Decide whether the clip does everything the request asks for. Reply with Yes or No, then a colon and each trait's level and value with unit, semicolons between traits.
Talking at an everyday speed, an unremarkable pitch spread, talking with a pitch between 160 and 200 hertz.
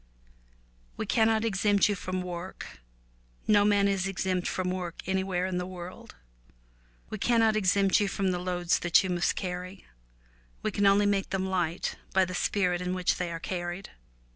No: average, 175 wpm; narrow, 1.9 semitones; medium, 185 Hz